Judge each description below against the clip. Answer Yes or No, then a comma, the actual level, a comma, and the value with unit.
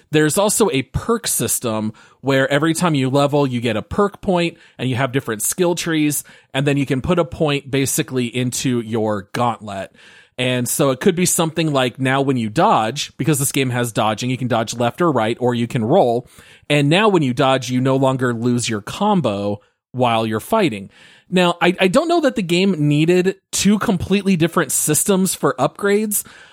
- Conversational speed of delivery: Yes, average, 195 wpm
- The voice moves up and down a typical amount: No, wide, 6.0 semitones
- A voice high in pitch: No, medium, 140 Hz